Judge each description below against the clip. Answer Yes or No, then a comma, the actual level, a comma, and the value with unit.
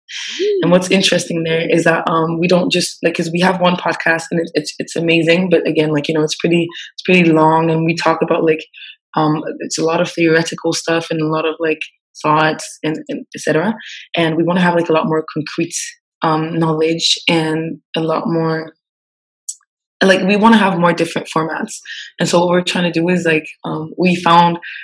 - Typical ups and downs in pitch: No, narrow, 1.6 semitones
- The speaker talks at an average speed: No, fast, 215 wpm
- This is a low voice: No, medium, 165 Hz